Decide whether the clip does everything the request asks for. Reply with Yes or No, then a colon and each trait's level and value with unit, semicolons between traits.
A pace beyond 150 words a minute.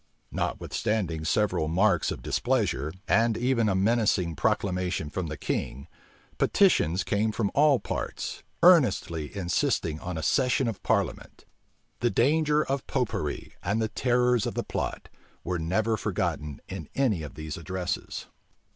No: average, 140 wpm